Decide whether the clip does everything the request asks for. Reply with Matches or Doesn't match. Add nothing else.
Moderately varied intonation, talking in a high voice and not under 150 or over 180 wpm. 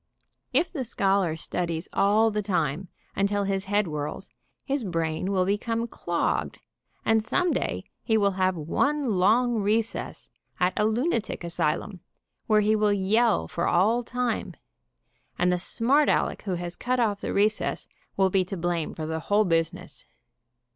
Matches